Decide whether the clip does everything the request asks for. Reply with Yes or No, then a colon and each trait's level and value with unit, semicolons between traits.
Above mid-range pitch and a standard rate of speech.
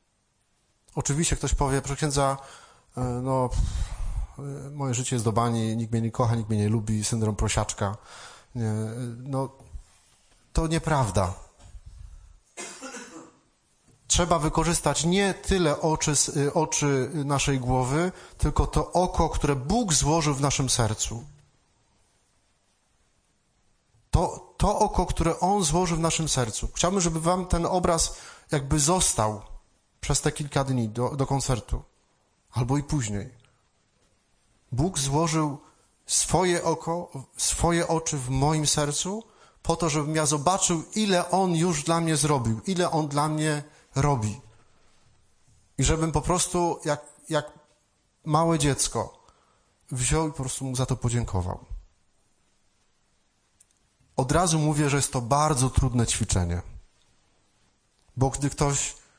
No: low, 135 Hz; average, 125 wpm